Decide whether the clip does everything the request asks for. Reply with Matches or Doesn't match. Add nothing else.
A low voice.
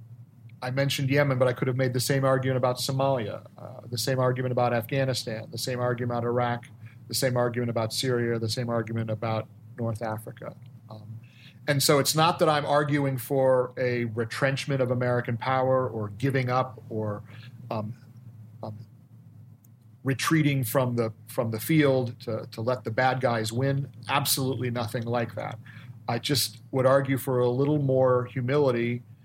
Matches